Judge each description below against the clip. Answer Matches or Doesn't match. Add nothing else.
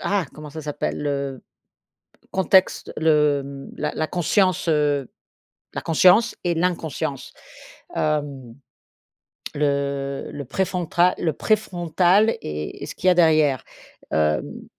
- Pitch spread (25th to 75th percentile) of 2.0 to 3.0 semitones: Doesn't match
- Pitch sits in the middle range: Matches